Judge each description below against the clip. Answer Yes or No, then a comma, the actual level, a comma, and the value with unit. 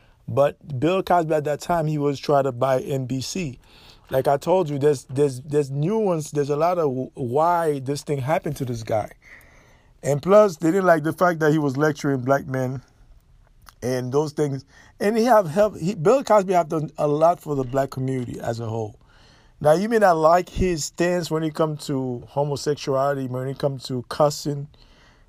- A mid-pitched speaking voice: Yes, medium, 145 Hz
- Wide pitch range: No, average, 3.5 semitones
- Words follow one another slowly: No, average, 195 wpm